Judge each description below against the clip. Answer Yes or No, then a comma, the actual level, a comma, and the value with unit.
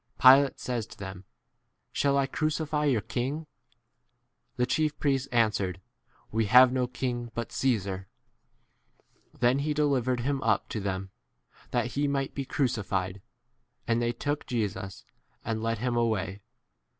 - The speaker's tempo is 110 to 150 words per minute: Yes, average, 140 wpm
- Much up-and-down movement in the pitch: No, average, 4.3 semitones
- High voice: No, low, 120 Hz